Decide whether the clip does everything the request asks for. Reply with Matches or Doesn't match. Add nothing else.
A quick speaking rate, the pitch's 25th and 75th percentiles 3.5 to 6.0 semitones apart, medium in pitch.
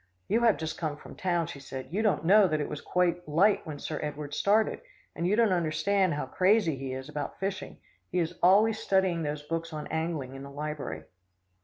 Matches